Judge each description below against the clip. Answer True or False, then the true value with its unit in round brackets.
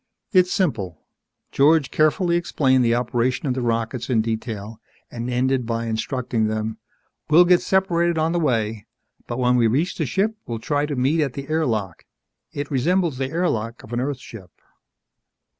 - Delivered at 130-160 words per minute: False (175 wpm)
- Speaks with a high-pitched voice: False (130 Hz)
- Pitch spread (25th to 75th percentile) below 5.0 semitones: False (5.4 semitones)